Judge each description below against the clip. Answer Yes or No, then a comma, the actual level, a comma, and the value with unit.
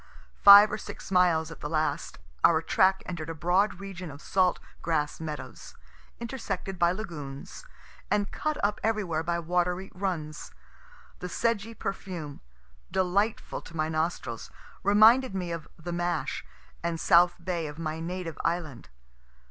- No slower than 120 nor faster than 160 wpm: Yes, average, 140 wpm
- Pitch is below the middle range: No, medium, 175 Hz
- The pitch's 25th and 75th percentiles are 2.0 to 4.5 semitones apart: Yes, average, 3.3 semitones